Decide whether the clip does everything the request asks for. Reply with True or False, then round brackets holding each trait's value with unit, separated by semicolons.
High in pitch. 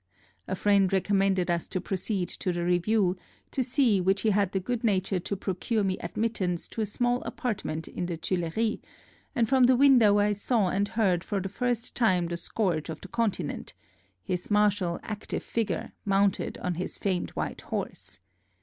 True (195 Hz)